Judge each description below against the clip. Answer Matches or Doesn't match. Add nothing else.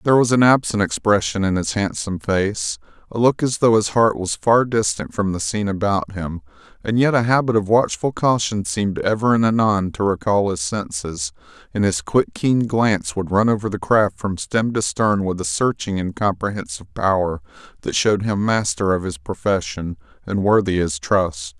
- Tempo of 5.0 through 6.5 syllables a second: Matches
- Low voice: Matches